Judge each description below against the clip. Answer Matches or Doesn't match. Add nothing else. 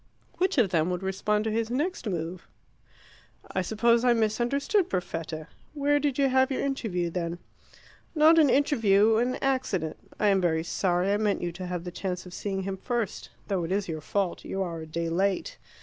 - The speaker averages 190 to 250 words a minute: Matches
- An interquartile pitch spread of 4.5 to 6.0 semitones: Matches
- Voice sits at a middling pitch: Doesn't match